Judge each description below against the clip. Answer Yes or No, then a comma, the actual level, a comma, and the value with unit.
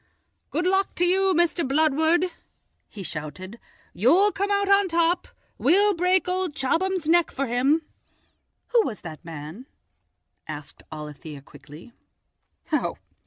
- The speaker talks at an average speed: No, slow, 120 wpm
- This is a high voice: Yes, very high, 320 Hz